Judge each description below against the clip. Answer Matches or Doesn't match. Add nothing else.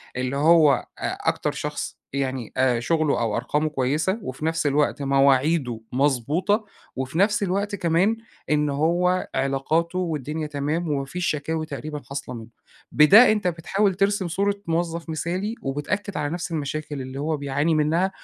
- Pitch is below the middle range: Doesn't match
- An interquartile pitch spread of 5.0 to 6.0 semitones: Doesn't match